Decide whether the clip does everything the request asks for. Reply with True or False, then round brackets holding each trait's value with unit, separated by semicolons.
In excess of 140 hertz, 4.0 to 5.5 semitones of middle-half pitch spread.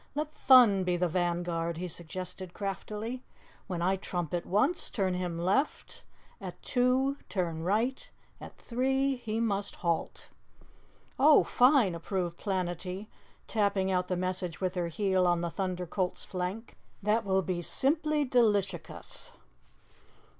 True (190 Hz; 4.5 semitones)